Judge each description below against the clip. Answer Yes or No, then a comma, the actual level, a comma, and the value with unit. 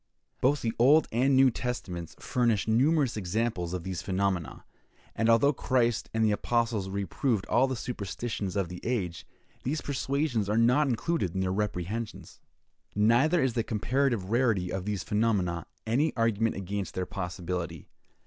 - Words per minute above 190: No, average, 150 wpm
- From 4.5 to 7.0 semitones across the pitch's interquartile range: Yes, average, 4.8 semitones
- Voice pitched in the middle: No, low, 110 Hz